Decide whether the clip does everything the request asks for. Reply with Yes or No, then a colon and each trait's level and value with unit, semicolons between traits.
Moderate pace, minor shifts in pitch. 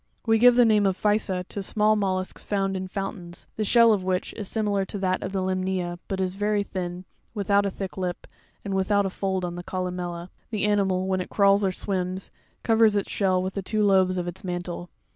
No: fast, 240 wpm; narrow, 1.8 semitones